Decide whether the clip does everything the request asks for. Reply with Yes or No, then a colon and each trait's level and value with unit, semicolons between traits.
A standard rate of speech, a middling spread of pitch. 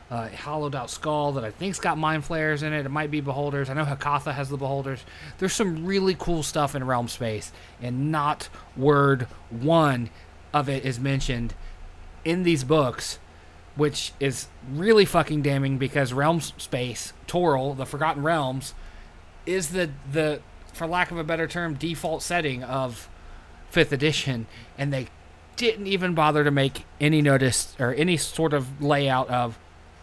Yes: average, 165 wpm; average, 4.5 semitones